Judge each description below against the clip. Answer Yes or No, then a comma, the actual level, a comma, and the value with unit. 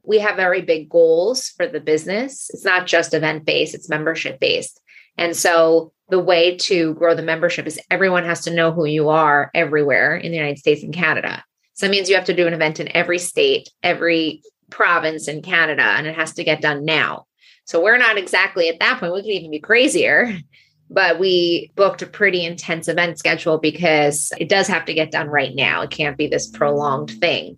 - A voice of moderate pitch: Yes, medium, 170 Hz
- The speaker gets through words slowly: No, fast, 205 wpm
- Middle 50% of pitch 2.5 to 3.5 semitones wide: Yes, average, 3.2 semitones